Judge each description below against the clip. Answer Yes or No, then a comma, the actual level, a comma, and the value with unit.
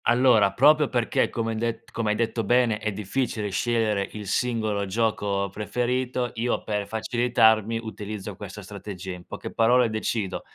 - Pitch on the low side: Yes, low, 110 Hz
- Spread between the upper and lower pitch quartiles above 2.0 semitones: Yes, narrow, 2.5 semitones